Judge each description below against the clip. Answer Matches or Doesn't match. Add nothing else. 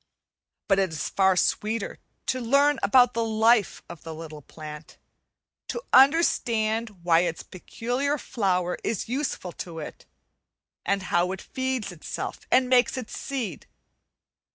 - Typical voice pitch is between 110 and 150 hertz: Doesn't match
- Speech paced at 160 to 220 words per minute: Doesn't match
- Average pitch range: Doesn't match